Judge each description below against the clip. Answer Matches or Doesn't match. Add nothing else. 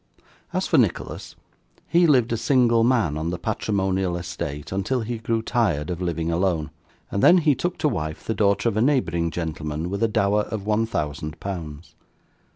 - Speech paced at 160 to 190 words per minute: Matches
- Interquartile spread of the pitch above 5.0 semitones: Matches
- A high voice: Doesn't match